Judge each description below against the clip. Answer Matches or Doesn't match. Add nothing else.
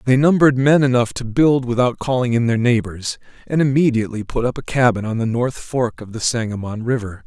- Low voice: Matches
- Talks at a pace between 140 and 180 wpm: Doesn't match